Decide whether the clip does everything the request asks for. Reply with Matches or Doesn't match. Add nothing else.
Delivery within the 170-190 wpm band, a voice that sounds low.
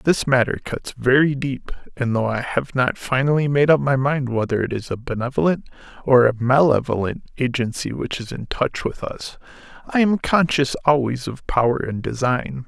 Matches